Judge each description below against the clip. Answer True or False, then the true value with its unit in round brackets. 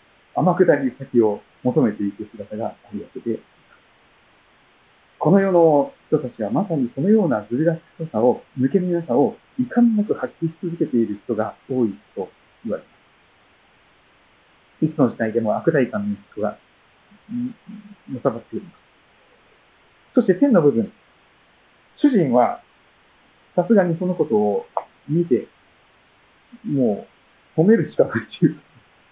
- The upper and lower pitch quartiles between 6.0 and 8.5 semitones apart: True (8.2 semitones)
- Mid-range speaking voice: True (170 Hz)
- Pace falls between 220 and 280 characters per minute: True (260 characters per minute)